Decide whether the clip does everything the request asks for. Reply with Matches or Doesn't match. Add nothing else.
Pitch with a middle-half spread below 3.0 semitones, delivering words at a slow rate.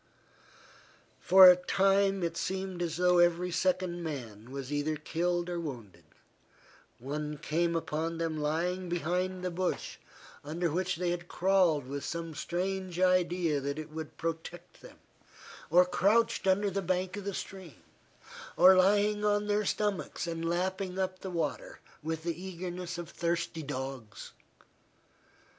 Doesn't match